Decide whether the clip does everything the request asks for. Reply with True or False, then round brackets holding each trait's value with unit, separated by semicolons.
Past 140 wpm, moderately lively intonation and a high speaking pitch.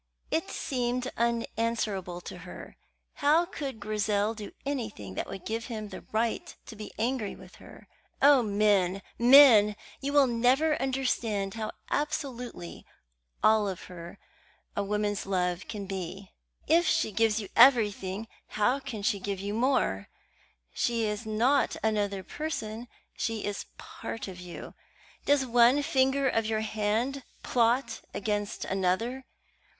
False (135 wpm; 3.9 semitones; 220 Hz)